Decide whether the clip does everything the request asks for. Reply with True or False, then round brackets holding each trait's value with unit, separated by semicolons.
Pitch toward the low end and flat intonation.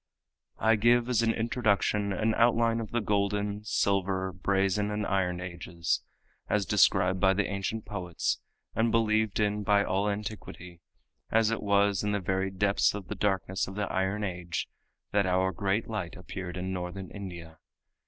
True (100 Hz; 2.1 semitones)